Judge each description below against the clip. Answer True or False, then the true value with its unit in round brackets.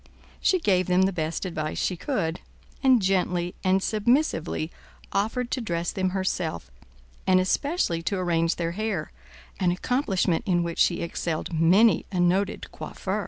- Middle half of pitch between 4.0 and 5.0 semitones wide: False (3.2 semitones)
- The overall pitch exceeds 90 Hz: True (185 Hz)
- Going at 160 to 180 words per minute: False (150 wpm)